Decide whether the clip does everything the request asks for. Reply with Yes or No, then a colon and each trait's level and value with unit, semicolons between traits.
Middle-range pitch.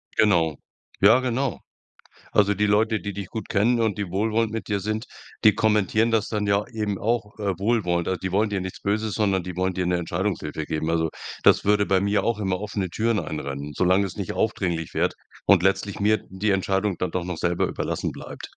No: low, 100 Hz